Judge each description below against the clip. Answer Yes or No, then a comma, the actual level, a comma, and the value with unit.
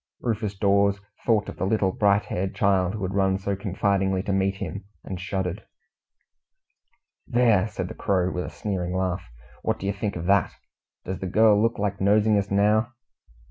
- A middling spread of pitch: No, narrow, 1.6 semitones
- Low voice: Yes, low, 100 Hz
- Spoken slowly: No, average, 180 wpm